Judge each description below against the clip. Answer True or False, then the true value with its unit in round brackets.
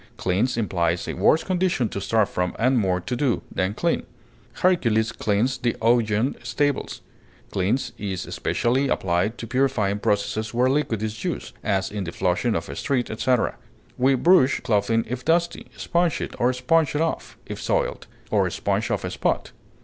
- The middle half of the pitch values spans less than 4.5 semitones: False (4.8 semitones)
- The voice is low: True (115 Hz)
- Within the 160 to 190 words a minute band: True (170 wpm)